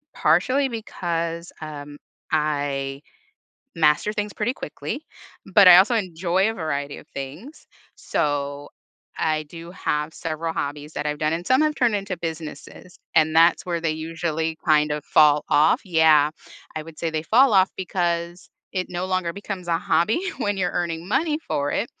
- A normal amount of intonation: Yes, average, 3.6 semitones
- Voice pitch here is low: No, medium, 165 Hz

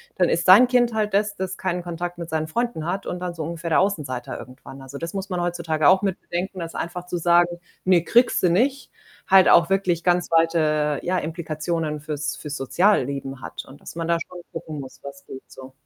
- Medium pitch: Yes, medium, 170 Hz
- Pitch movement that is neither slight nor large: Yes, average, 3.2 semitones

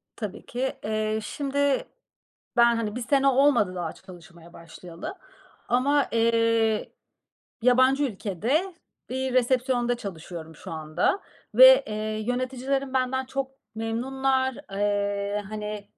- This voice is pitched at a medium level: No, high, 230 Hz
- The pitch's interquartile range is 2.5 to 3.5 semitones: No, average, 4.3 semitones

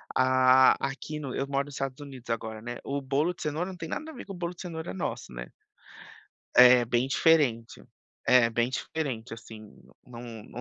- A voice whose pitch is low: Yes, low, 130 Hz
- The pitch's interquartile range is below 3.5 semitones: No, average, 4.3 semitones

